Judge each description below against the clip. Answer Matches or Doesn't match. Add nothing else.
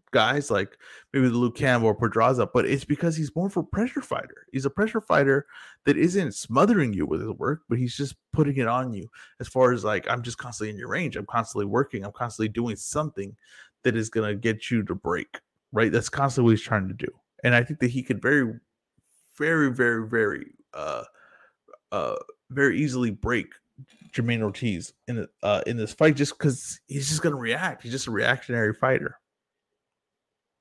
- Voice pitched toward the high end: Doesn't match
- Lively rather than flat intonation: Doesn't match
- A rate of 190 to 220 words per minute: Matches